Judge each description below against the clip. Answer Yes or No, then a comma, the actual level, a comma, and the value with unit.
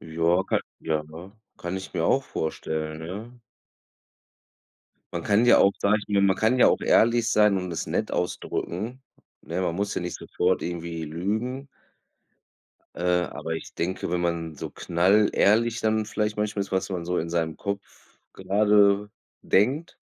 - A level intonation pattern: No, average, 3.8 semitones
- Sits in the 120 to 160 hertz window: No, very low, 95 Hz